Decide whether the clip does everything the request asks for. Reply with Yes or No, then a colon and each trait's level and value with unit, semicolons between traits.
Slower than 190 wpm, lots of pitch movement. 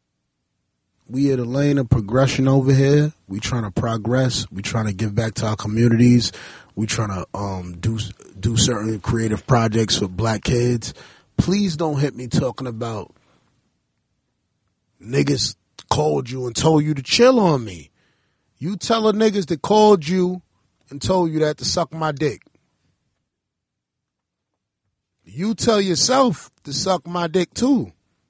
Yes: average, 150 wpm; wide, 7.1 semitones